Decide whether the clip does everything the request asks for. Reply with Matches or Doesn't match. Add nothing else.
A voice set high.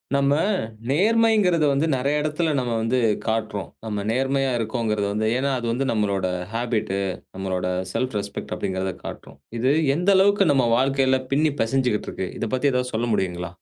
Doesn't match